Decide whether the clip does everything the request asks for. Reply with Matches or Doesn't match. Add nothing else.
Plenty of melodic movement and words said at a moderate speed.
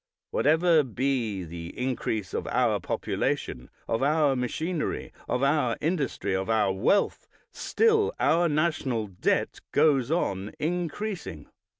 Doesn't match